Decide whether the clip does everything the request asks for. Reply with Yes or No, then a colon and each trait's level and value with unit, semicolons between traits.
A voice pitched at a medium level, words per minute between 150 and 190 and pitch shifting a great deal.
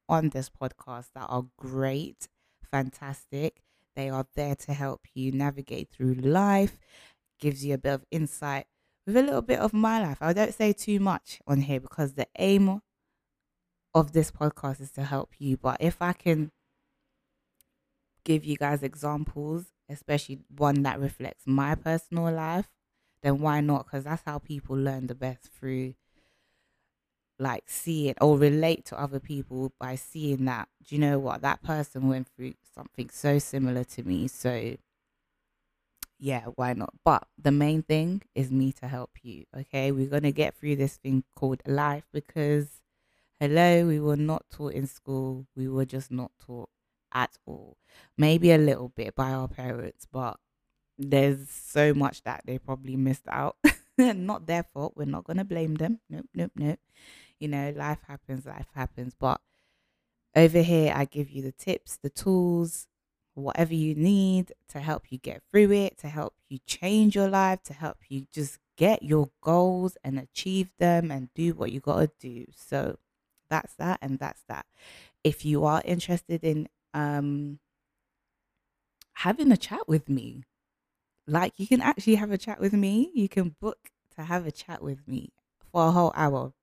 No: medium, 145 Hz; average, 170 wpm; average, 3.5 semitones